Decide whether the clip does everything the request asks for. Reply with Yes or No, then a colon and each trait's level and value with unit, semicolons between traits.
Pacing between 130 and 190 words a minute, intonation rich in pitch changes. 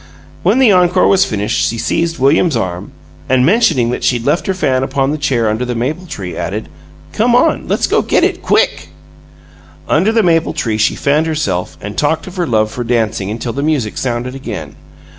No: average, 200 wpm; wide, 6.3 semitones